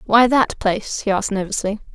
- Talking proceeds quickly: No, average, 185 wpm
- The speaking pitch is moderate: No, high, 215 Hz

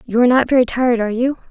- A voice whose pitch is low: No, high, 245 Hz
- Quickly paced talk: Yes, fast, 280 wpm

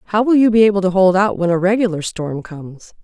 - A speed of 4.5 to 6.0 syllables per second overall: No, 6.3 syllables/s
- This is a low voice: No, high, 195 Hz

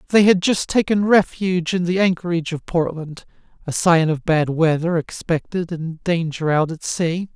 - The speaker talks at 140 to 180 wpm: Yes, average, 165 wpm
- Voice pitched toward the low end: No, medium, 170 Hz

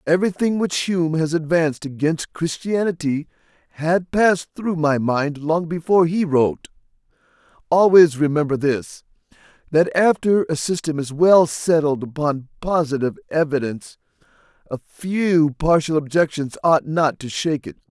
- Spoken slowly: Yes, slow, 130 wpm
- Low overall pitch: No, medium, 160 Hz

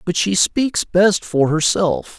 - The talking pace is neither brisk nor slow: Yes, average, 165 wpm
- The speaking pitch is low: No, medium, 185 Hz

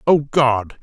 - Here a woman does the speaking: No, male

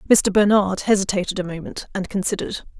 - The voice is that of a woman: Yes, female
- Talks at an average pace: Yes, average, 150 wpm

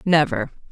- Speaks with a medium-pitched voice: Yes, medium, 145 Hz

